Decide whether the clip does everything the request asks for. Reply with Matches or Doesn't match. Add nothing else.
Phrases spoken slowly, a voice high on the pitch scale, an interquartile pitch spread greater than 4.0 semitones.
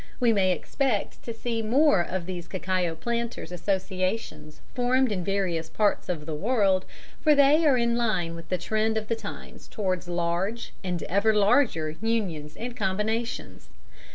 Doesn't match